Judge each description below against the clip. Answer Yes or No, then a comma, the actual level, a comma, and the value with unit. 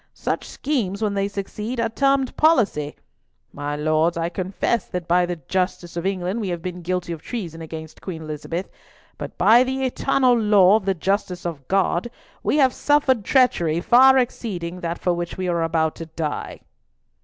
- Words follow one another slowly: No, average, 180 wpm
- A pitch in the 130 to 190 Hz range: Yes, medium, 185 Hz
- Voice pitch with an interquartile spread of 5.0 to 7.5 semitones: Yes, wide, 5.4 semitones